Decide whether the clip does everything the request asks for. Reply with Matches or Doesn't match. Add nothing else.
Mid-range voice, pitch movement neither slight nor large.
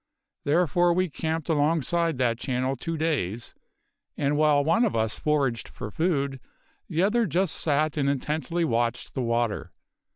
Matches